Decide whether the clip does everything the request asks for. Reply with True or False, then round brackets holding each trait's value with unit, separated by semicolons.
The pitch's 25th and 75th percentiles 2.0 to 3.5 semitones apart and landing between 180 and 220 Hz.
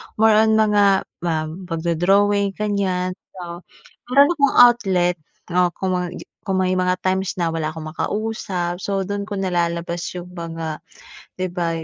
True (2.8 semitones; 185 Hz)